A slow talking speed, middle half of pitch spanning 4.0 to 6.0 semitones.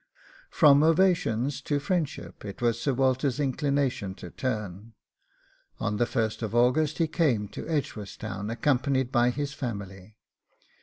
Yes: slow, 125 wpm; average, 4.8 semitones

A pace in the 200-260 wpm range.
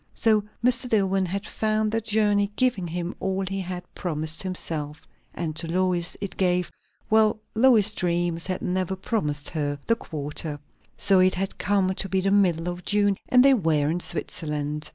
No: average, 175 wpm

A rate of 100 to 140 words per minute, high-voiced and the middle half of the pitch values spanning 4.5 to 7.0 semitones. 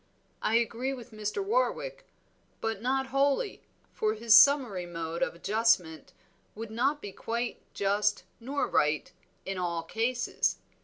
Yes: slow, 135 wpm; high, 225 Hz; average, 5.2 semitones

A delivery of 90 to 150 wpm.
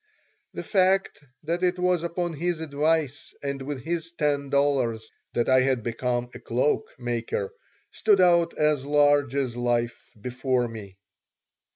Yes: average, 145 wpm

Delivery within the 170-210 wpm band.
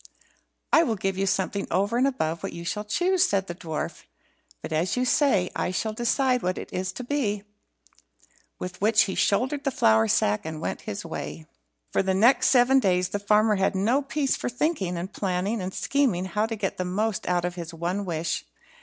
Yes: fast, 205 wpm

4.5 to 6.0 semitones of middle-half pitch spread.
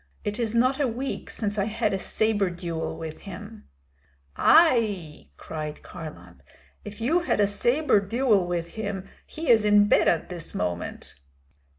Yes: average, 5.0 semitones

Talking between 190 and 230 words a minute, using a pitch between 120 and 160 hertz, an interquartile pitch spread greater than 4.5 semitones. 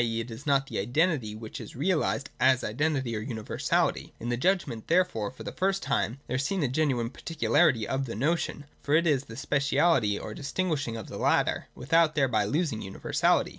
Yes: average, 195 wpm; low, 135 Hz; wide, 5.5 semitones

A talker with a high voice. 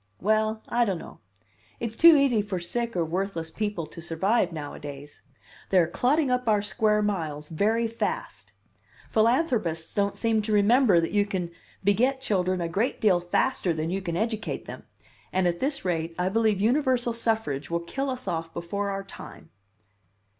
Yes: high, 200 Hz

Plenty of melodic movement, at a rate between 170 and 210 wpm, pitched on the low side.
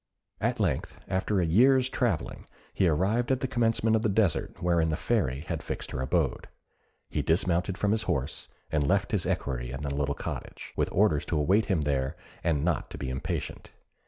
Yes: wide, 6.7 semitones; average, 190 wpm; very low, 85 Hz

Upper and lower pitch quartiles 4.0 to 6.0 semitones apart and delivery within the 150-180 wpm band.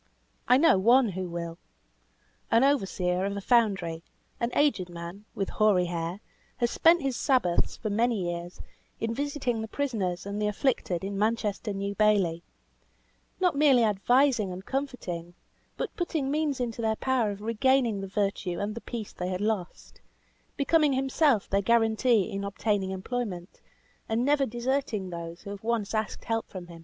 Yes: average, 4.8 semitones; average, 165 wpm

